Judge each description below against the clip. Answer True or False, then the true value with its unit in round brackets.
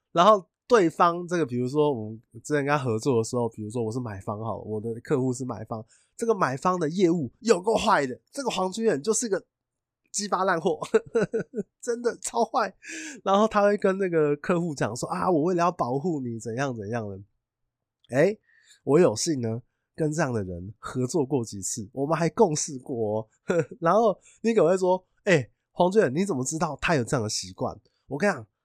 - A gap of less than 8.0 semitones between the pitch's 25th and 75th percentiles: False (8.6 semitones)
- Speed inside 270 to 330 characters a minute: True (290 characters per minute)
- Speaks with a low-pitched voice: False (155 Hz)